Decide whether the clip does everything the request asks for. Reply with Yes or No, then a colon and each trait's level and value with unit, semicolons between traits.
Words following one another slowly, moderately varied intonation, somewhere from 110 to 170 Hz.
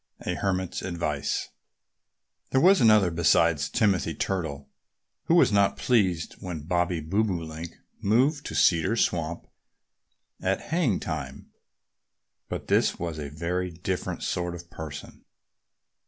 No: slow, 125 wpm; average, 3.8 semitones; very low, 90 Hz